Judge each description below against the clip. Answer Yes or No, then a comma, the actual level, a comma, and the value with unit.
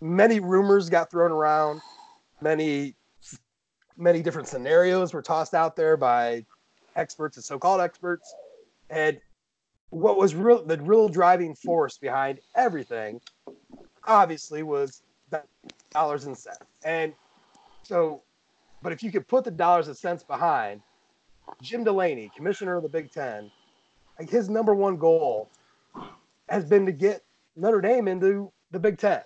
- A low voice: No, medium, 175 Hz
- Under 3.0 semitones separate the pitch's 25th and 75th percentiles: No, average, 4.7 semitones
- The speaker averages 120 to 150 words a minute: Yes, average, 140 wpm